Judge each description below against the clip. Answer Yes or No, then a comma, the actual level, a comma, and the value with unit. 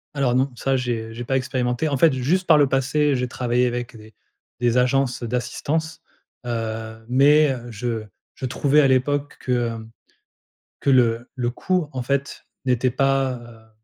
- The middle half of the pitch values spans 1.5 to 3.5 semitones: Yes, narrow, 2.5 semitones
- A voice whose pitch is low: Yes, low, 125 Hz